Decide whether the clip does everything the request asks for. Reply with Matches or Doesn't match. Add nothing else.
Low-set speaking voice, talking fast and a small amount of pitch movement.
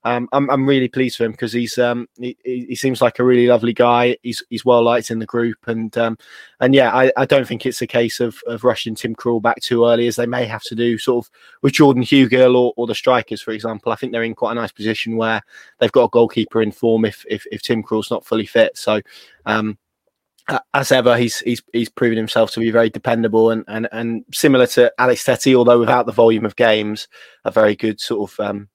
Matches